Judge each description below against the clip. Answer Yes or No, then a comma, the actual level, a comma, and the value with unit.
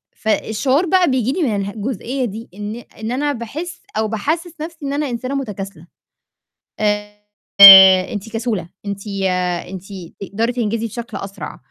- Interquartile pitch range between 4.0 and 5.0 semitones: Yes, average, 4.6 semitones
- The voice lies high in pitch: Yes, high, 225 Hz